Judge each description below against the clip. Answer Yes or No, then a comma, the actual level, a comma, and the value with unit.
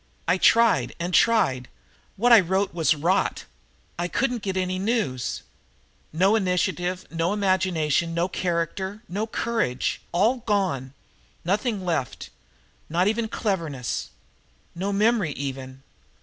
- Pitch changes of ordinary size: Yes, average, 3.9 semitones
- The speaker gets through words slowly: Yes, slow, 120 wpm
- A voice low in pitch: No, medium, 185 Hz